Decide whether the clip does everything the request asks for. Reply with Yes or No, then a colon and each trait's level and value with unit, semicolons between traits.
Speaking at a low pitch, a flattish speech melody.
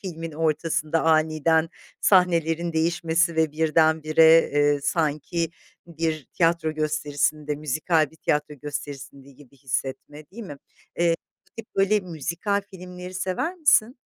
No: medium, 160 Hz; narrow, 2.3 semitones